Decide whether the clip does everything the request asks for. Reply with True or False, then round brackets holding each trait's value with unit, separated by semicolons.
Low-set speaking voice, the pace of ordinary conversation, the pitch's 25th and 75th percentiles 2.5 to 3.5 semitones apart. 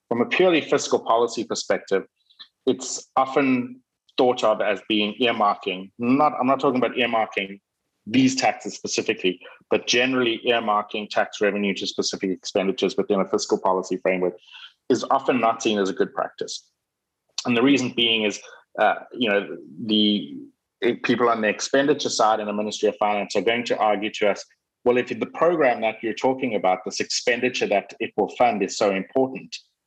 False (115 Hz; 175 wpm; 3.9 semitones)